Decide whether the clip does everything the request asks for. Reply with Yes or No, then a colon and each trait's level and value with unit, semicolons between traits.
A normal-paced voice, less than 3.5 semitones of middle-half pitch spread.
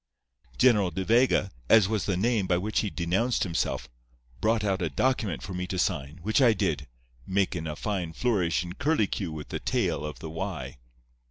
No: average, 185 wpm; average, 4.4 semitones